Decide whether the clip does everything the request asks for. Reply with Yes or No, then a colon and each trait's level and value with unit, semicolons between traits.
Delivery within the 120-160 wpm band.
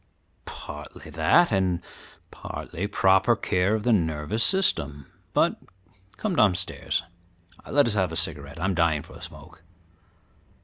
Yes: average, 140 wpm